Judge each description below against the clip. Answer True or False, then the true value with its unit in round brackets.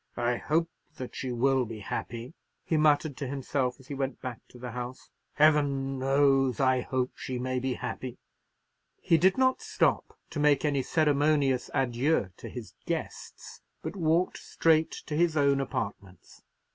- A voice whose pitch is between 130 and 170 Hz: True (135 Hz)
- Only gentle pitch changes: False (3.0 semitones)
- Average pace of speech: True (160 wpm)